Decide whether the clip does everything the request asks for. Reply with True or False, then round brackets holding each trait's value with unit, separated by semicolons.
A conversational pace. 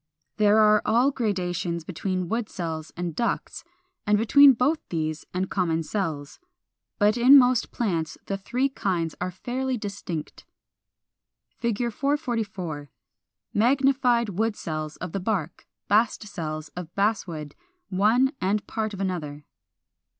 False (130 wpm)